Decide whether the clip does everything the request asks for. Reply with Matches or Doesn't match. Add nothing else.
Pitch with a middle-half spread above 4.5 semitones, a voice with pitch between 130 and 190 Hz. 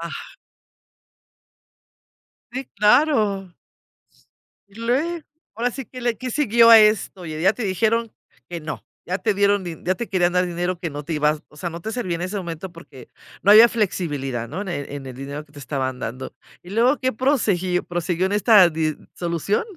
Matches